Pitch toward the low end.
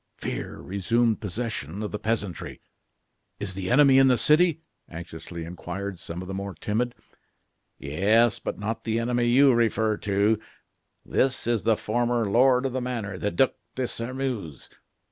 Yes: low, 110 Hz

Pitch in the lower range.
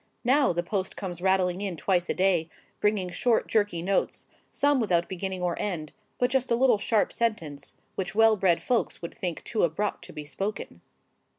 No: high, 190 Hz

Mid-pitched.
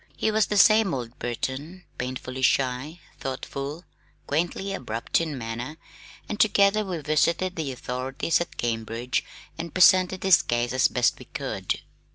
Yes: medium, 145 Hz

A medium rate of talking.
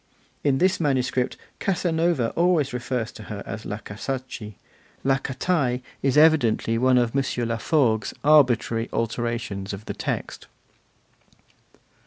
No: slow, 120 wpm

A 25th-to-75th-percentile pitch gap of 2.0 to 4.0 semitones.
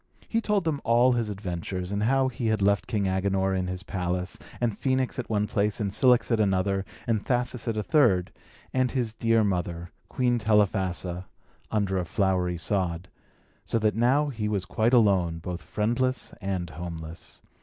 No: average, 4.4 semitones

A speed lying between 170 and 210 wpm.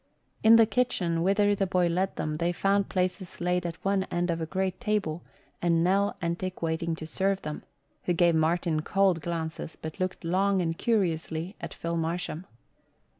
Yes: average, 175 wpm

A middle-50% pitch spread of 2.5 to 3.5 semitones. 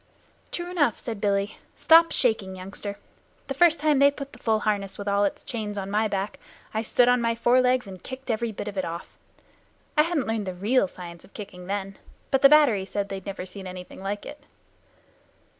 No: average, 4.6 semitones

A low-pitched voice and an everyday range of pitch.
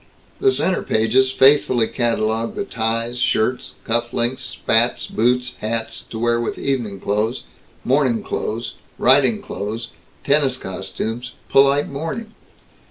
Yes: low, 120 Hz; average, 3.0 semitones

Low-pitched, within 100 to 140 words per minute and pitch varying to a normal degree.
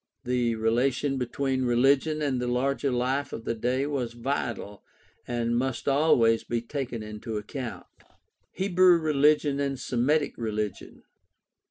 Yes: low, 125 Hz; slow, 135 wpm; average, 3.2 semitones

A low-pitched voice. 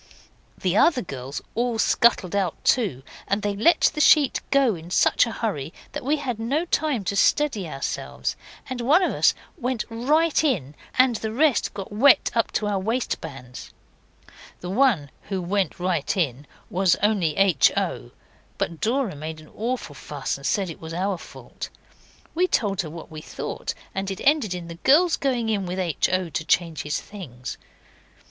No: high, 200 Hz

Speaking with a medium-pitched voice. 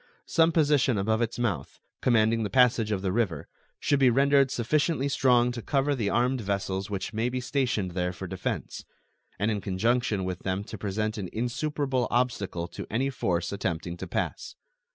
No: low, 115 Hz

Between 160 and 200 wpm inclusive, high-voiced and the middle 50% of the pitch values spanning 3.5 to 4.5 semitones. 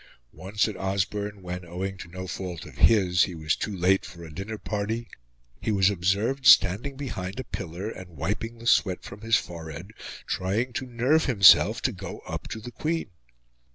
No: average, 185 wpm; low, 100 Hz; average, 3.9 semitones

